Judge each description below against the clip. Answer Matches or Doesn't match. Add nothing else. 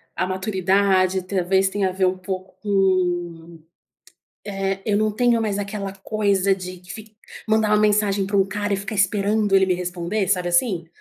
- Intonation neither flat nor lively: Doesn't match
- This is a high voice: Matches